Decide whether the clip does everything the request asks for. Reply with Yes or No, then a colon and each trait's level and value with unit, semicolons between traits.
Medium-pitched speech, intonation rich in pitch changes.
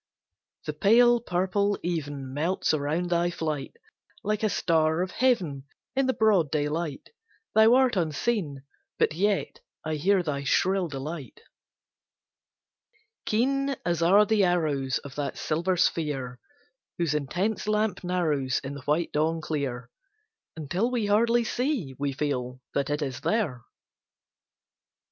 Yes: medium, 170 Hz; wide, 6.1 semitones